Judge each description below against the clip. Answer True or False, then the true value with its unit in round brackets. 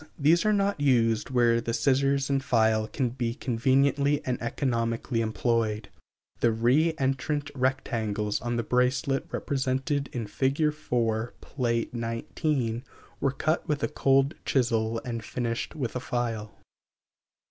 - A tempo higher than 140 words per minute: False (135 wpm)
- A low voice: True (125 Hz)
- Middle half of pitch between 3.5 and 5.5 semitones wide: False (3.1 semitones)